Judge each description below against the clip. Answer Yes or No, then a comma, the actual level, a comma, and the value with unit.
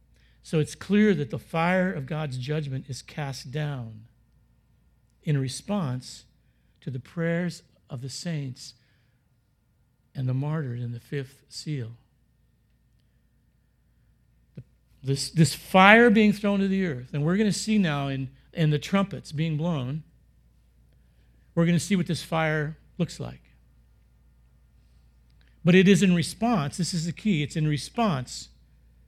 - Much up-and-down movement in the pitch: Yes, wide, 5.7 semitones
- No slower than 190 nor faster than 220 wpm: No, average, 140 wpm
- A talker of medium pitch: Yes, medium, 145 Hz